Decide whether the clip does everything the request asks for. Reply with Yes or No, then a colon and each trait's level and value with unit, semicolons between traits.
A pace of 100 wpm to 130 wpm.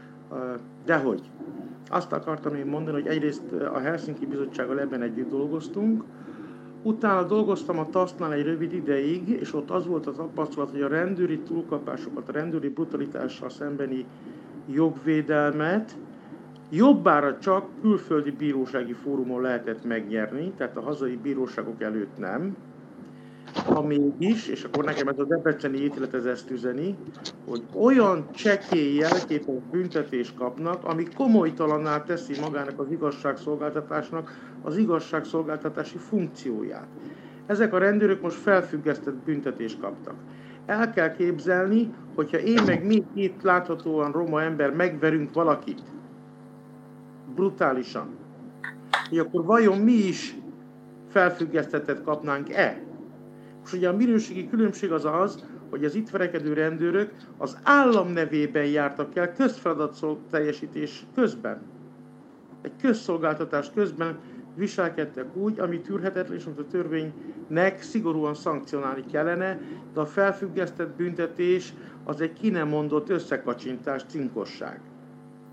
Yes: average, 115 wpm